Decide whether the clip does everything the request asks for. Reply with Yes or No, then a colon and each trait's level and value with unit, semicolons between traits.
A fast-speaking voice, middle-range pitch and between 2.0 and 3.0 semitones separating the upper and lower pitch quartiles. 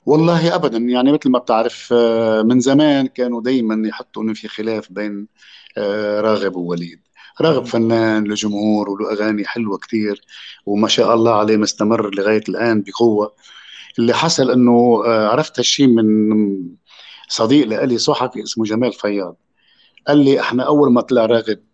No: fast, 140 wpm; low, 110 Hz; narrow, 2.6 semitones